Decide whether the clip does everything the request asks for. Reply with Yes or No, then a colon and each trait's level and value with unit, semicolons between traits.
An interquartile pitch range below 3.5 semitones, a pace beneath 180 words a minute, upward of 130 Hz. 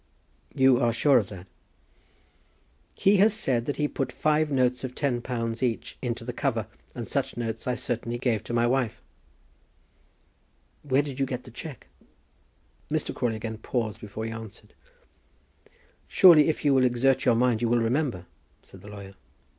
No: average, 3.0 semitones; average, 170 wpm; low, 125 Hz